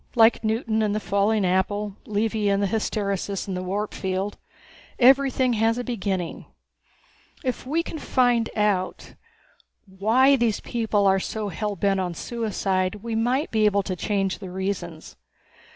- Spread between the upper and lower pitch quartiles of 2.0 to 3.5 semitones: Yes, average, 2.9 semitones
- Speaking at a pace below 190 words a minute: Yes, average, 150 wpm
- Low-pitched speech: No, high, 210 Hz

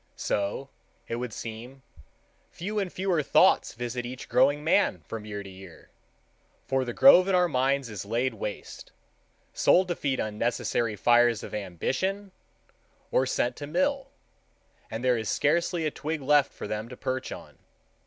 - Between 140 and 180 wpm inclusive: Yes, average, 155 wpm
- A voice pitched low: Yes, low, 130 Hz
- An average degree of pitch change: No, wide, 6.1 semitones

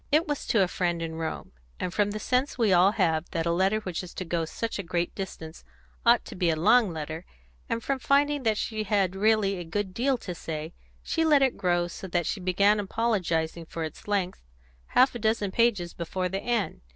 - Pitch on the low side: No, high, 195 Hz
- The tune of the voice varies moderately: Yes, average, 4.7 semitones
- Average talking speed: No, fast, 220 wpm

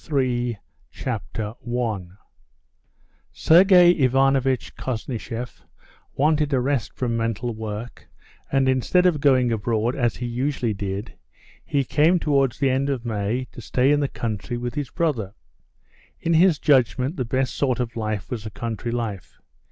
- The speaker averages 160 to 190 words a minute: No, average, 150 wpm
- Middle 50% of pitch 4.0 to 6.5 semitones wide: No, average, 3.4 semitones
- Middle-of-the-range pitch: No, low, 125 Hz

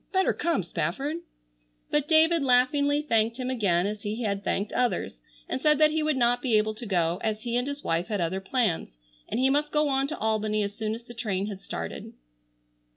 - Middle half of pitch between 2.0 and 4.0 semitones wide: No, wide, 5.5 semitones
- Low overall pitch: No, high, 235 Hz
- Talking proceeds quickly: Yes, fast, 215 wpm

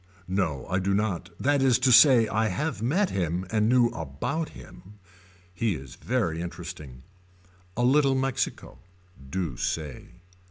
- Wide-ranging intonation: Yes, wide, 7.2 semitones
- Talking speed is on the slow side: No, average, 145 wpm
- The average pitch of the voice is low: Yes, low, 105 Hz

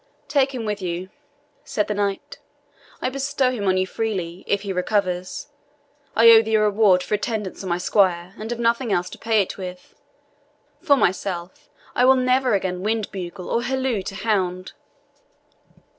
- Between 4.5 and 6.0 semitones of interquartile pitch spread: No, average, 3.9 semitones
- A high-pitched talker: Yes, high, 205 Hz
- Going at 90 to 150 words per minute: No, average, 175 wpm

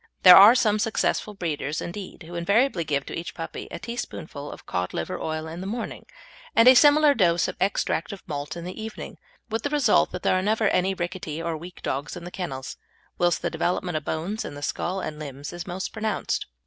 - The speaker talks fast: Yes, fast, 220 wpm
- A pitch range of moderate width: Yes, average, 5.0 semitones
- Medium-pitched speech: Yes, medium, 180 Hz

